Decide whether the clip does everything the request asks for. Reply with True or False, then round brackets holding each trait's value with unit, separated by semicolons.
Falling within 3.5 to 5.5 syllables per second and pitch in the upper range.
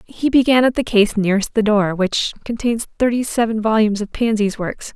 True (5.4 syllables/s; 220 Hz)